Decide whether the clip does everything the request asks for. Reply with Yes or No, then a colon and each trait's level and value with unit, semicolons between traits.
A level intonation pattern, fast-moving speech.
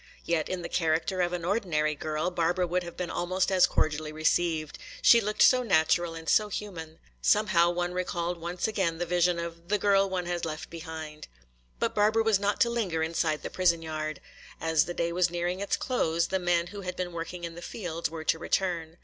Yes: narrow, 2.1 semitones; fast, 210 wpm